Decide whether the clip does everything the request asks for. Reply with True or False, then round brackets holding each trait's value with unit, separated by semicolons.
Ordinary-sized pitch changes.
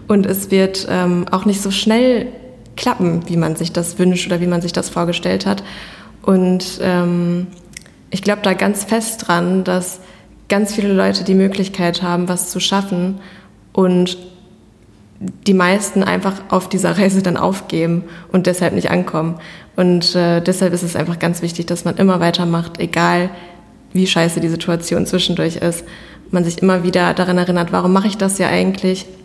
False (1.8 semitones)